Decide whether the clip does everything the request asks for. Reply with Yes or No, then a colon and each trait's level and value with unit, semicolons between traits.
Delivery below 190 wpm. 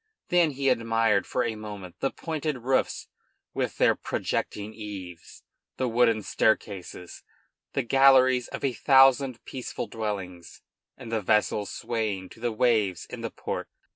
Yes: average, 140 wpm